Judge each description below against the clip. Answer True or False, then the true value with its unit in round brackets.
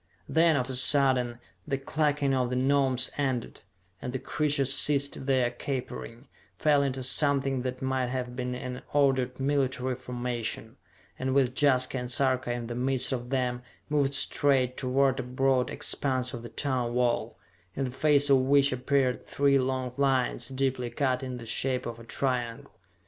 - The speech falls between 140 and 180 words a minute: True (165 wpm)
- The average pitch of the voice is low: True (130 Hz)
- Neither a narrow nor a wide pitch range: False (1.7 semitones)